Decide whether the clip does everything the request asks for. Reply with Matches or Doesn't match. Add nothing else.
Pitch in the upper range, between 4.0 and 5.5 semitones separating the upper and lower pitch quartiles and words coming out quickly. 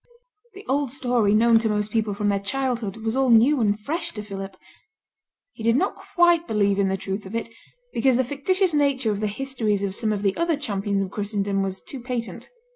Matches